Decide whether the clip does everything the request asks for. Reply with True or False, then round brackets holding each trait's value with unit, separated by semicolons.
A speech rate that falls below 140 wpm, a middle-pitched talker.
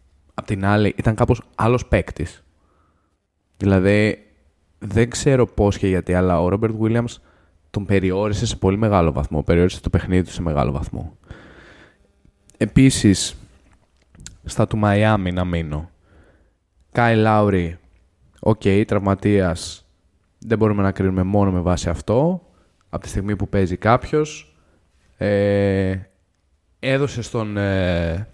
False (120 wpm; 95 Hz)